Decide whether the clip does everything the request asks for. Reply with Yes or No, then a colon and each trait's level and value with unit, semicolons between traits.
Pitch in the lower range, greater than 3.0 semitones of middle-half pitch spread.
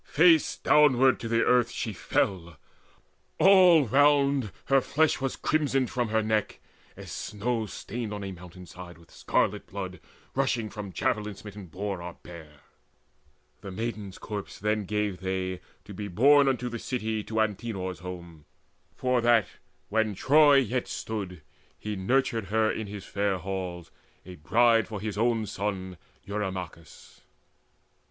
Yes: low, 105 Hz; average, 4.5 semitones